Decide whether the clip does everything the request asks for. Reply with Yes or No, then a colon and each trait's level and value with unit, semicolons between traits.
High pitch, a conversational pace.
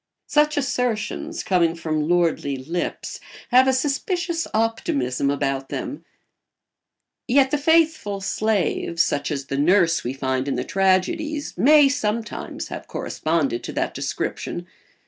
No: high, 195 Hz; slow, 125 wpm